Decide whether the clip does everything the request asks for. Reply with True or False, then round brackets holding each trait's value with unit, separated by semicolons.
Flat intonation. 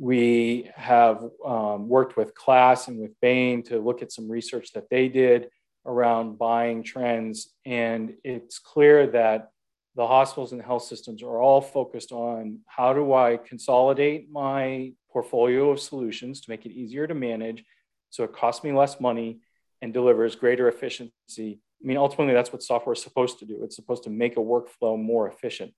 True (2.0 semitones)